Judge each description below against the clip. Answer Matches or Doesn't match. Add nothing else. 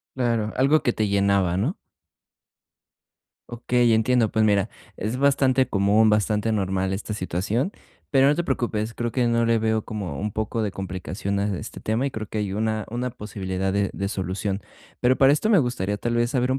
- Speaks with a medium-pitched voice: Doesn't match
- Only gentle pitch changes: Doesn't match